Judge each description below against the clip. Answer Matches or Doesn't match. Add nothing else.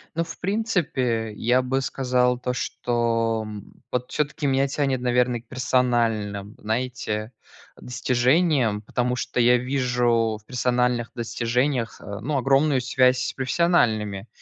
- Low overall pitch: Matches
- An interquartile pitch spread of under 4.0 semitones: Matches